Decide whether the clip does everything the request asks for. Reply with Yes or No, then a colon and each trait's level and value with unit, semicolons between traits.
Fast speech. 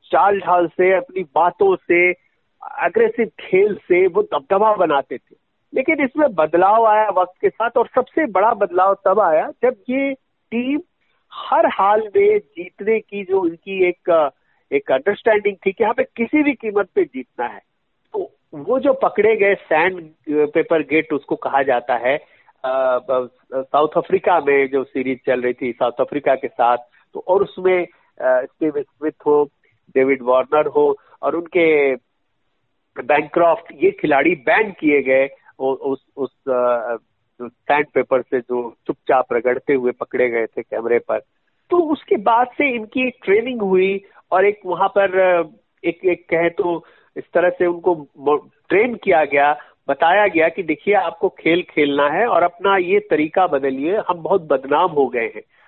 No: average, 155 wpm